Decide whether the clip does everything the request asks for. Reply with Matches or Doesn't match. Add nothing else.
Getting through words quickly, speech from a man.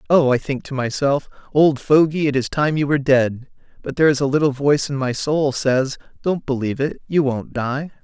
Matches